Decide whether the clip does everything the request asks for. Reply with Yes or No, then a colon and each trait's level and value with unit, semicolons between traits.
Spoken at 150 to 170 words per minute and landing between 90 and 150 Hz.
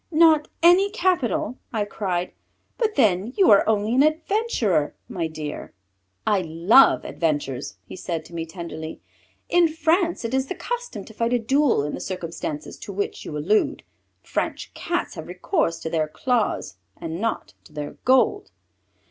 No: average, 160 wpm; high, 215 Hz